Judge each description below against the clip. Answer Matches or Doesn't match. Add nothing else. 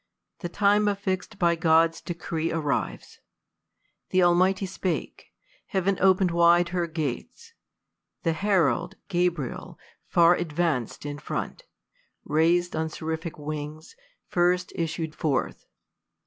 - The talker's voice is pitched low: Doesn't match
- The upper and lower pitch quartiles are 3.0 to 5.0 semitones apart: Doesn't match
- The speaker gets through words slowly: Matches